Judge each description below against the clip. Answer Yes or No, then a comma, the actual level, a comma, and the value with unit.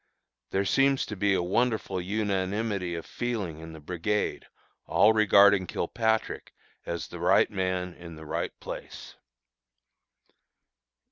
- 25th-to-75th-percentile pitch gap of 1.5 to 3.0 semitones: No, average, 3.5 semitones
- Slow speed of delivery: Yes, slow, 125 wpm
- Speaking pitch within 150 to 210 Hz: No, very low, 95 Hz